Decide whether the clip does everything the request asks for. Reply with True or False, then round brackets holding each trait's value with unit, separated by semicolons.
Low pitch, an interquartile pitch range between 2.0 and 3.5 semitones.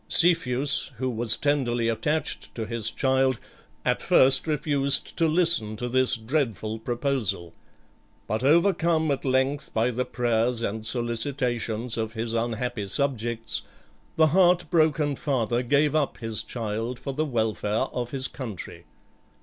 False (125 Hz; 4.1 semitones)